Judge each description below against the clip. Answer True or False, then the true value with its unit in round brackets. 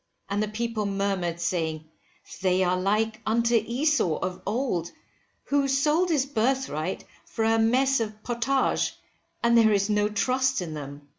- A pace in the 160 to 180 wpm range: False (150 wpm)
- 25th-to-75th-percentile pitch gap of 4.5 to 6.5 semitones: True (5.4 semitones)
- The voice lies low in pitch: False (220 Hz)